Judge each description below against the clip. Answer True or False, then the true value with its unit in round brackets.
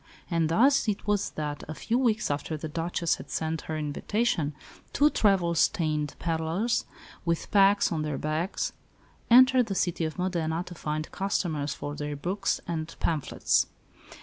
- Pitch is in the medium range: True (165 Hz)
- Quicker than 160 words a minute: False (155 wpm)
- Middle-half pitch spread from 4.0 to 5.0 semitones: True (4.4 semitones)